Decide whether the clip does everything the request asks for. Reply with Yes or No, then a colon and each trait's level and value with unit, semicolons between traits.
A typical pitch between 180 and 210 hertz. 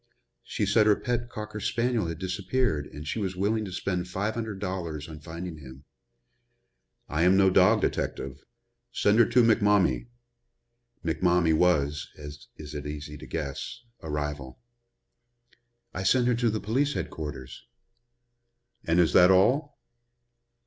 No: very low, 90 Hz